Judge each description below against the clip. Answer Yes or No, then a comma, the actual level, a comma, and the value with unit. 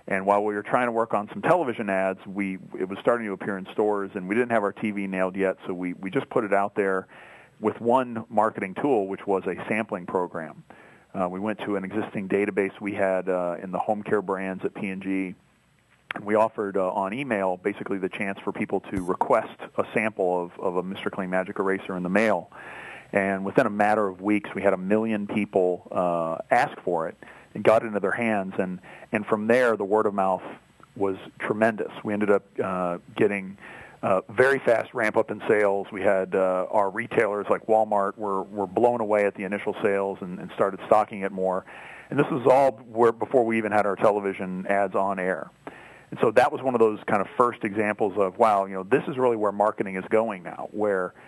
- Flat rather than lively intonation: Yes, narrow, 2.2 semitones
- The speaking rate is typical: No, fast, 220 wpm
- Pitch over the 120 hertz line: No, low, 100 Hz